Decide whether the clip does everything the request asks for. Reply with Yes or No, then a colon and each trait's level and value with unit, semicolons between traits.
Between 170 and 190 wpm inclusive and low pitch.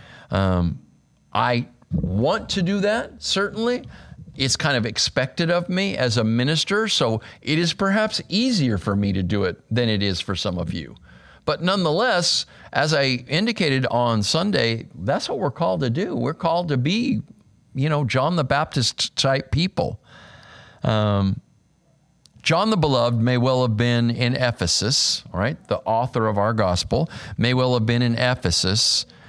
No: average, 160 wpm; low, 125 Hz